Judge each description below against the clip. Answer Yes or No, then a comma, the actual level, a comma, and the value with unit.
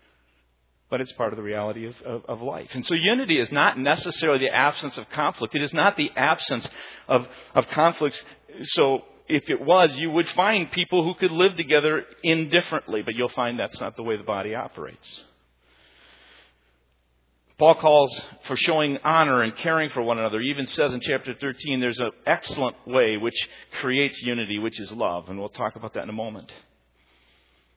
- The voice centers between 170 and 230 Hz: No, low, 125 Hz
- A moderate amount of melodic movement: No, wide, 7.2 semitones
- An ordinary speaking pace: Yes, average, 185 wpm